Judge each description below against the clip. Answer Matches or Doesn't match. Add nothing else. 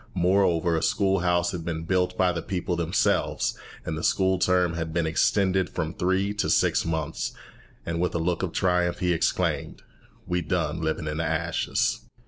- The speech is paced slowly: Doesn't match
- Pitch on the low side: Matches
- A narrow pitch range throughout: Matches